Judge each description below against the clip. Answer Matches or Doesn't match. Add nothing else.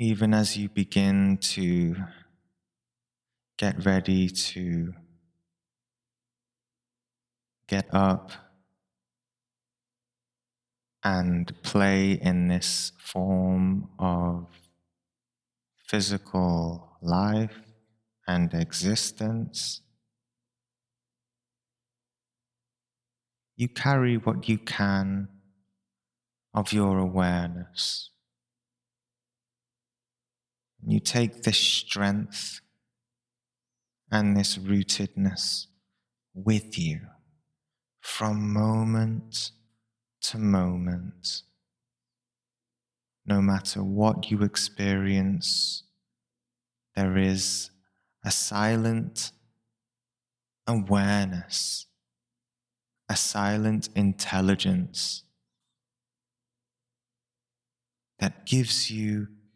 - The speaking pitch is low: Matches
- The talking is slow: Matches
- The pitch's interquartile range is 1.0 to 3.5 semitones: Doesn't match